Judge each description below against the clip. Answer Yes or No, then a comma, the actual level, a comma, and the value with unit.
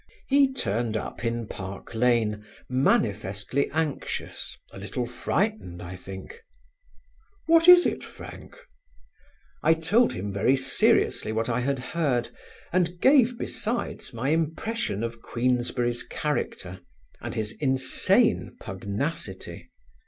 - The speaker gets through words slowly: Yes, slow, 115 wpm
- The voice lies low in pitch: Yes, low, 125 Hz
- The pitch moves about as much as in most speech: No, wide, 7.4 semitones